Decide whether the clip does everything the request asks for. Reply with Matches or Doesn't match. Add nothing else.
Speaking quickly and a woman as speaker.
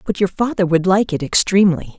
Matches